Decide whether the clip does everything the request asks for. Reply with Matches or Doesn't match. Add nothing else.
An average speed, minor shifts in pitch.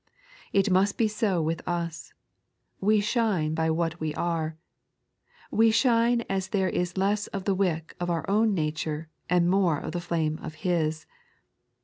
Doesn't match